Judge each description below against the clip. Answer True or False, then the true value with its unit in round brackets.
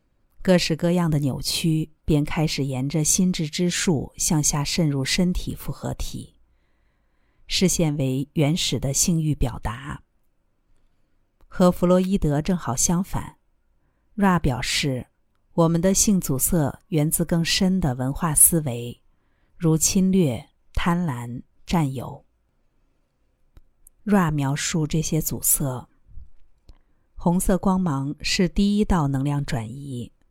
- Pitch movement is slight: False (5.2 semitones)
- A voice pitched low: False (155 Hz)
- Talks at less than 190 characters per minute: True (180 characters per minute)